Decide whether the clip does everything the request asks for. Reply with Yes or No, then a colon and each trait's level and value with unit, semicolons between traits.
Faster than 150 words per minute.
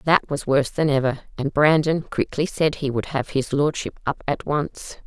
Yes: average, 200 wpm